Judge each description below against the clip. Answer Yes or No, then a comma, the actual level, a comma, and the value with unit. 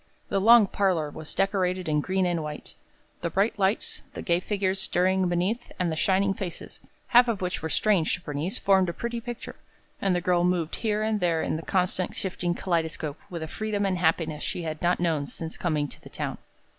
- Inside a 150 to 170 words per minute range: No, fast, 205 wpm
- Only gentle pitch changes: No, average, 3.1 semitones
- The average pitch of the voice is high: No, medium, 180 Hz